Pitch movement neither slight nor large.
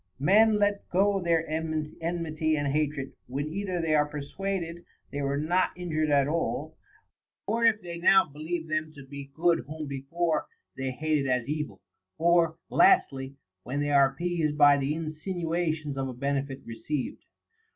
Yes: average, 3.4 semitones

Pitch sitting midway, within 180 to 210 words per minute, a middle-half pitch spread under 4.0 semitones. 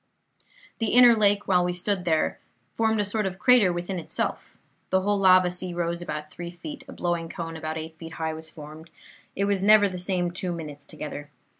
Yes: medium, 180 Hz; average, 200 wpm; average, 3.4 semitones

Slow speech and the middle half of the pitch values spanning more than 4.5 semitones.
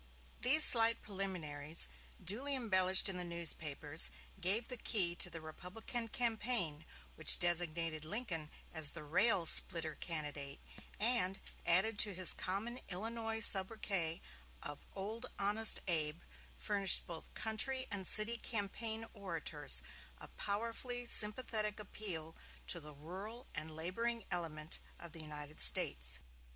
Yes: slow, 125 wpm; wide, 5.6 semitones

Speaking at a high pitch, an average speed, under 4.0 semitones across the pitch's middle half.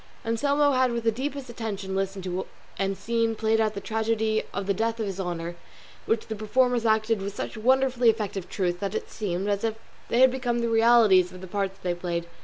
No: high, 220 Hz; fast, 210 wpm; average, 3.2 semitones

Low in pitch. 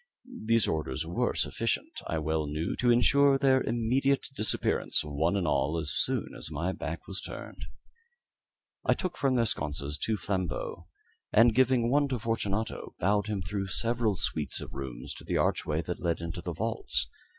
Yes: low, 100 Hz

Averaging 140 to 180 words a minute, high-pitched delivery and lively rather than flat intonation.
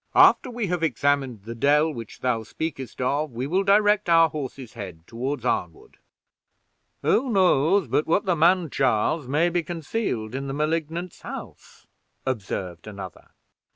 No: average, 150 wpm; medium, 150 Hz; wide, 5.9 semitones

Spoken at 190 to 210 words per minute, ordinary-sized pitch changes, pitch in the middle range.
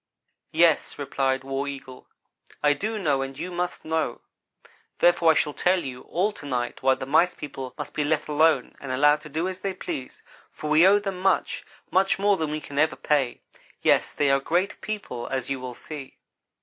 Yes: average, 200 wpm; average, 4.7 semitones; medium, 150 Hz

